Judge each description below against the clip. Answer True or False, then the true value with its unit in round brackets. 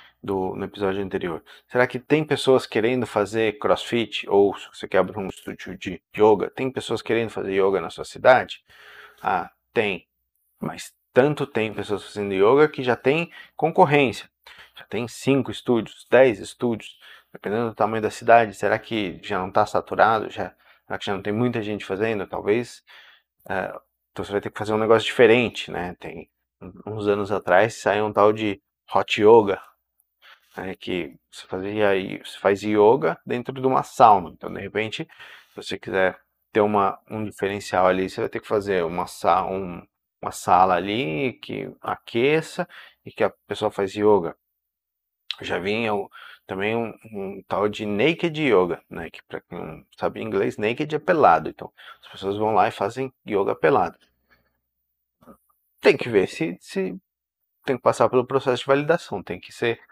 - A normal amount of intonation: True (4.0 semitones)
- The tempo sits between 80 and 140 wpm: False (170 wpm)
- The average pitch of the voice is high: False (105 Hz)